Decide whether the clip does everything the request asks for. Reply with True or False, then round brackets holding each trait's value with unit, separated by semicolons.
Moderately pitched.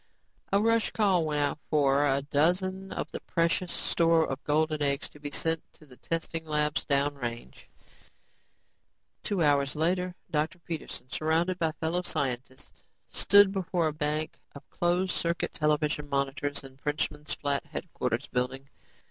True (155 Hz)